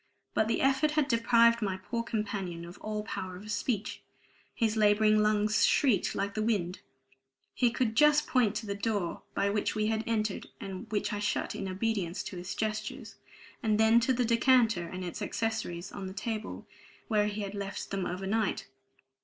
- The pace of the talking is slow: No, average, 180 wpm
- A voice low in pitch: No, high, 215 Hz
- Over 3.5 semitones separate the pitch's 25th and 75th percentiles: No, narrow, 2.5 semitones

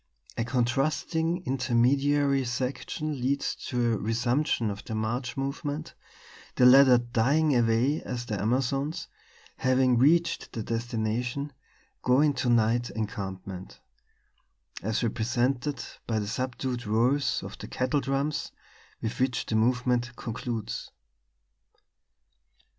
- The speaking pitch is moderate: No, low, 125 Hz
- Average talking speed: No, slow, 110 wpm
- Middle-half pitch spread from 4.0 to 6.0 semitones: No, average, 3.1 semitones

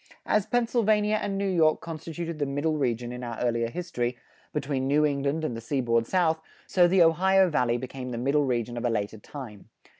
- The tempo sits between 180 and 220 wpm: Yes, average, 190 wpm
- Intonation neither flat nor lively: No, wide, 6.0 semitones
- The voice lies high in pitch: No, medium, 145 Hz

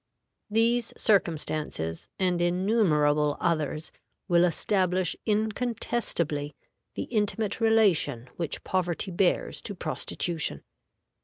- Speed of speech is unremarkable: No, slow, 85 wpm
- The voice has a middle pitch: Yes, medium, 180 Hz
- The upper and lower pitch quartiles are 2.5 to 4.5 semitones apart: No, wide, 5.4 semitones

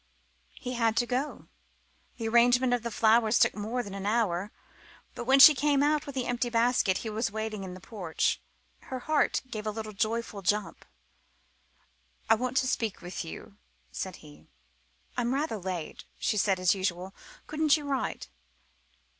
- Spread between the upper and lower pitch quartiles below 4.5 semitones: Yes, average, 4.0 semitones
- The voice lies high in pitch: Yes, high, 225 Hz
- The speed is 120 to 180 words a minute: Yes, average, 170 wpm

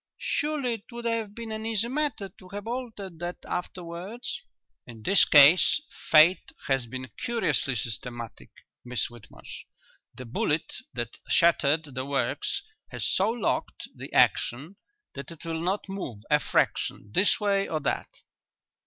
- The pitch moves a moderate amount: No, wide, 8.4 semitones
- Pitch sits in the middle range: Yes, medium, 175 Hz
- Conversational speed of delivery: Yes, average, 145 wpm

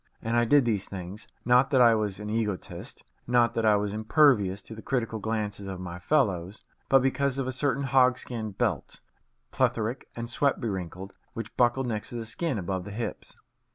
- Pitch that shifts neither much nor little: Yes, average, 3.7 semitones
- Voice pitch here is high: No, low, 115 Hz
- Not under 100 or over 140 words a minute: No, average, 185 wpm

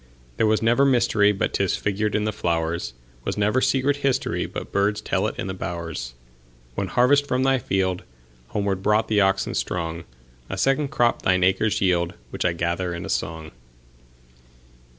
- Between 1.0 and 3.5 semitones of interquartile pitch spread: No, average, 4.9 semitones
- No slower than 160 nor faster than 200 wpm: No, average, 145 wpm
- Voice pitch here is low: Yes, very low, 95 Hz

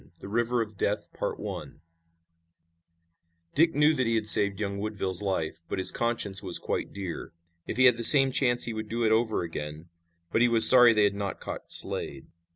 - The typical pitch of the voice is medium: No, low, 110 Hz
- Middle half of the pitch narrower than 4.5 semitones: Yes, average, 3.3 semitones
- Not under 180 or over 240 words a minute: Yes, average, 190 wpm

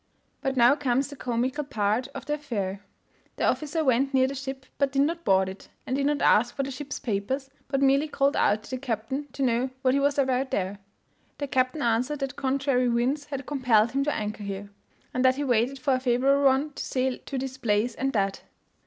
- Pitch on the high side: Yes, very high, 265 Hz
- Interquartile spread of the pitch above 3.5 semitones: No, average, 2.7 semitones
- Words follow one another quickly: Yes, fast, 220 wpm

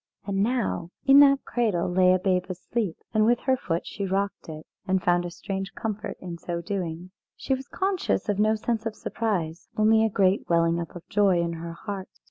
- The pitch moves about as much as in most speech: Yes, average, 3.9 semitones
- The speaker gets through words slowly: No, fast, 205 wpm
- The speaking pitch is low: No, high, 195 Hz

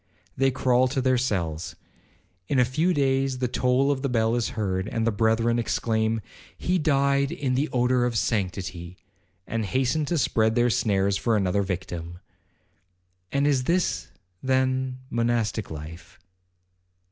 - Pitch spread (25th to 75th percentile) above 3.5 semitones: Yes, average, 4.6 semitones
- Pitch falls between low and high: No, low, 120 Hz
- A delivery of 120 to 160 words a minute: Yes, average, 145 wpm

